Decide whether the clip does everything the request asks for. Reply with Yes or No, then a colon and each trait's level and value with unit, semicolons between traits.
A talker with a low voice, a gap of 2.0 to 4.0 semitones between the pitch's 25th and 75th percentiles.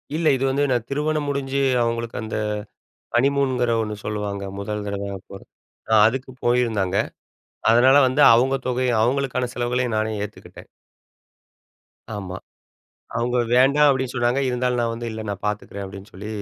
Yes: low, 120 Hz; average, 3.6 semitones